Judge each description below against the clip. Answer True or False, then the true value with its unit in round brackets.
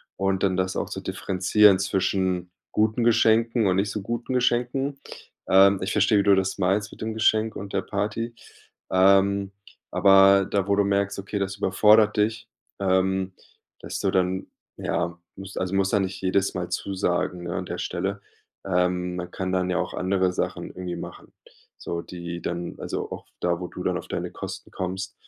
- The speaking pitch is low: True (95 Hz)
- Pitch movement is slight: True (1.9 semitones)